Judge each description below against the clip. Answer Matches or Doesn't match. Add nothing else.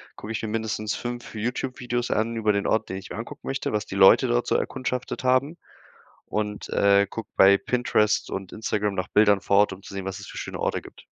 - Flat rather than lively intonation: Doesn't match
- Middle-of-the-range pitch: Doesn't match